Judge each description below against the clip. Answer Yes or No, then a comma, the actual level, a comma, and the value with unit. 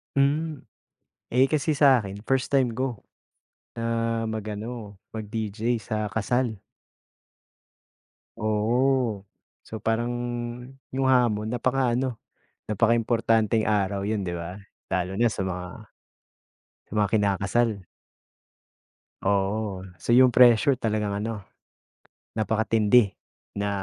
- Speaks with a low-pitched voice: Yes, low, 110 Hz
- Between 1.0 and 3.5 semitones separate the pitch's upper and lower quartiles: Yes, average, 2.9 semitones